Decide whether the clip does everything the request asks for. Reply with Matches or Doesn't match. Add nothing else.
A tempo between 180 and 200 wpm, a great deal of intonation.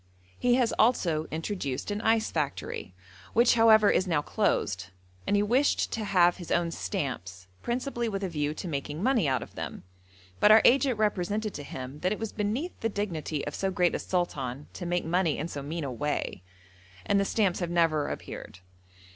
Matches